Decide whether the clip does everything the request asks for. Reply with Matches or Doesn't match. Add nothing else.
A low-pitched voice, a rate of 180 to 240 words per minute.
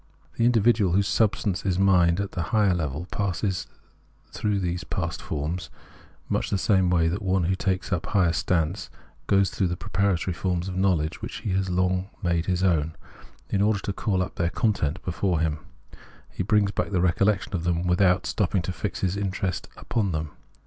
Matches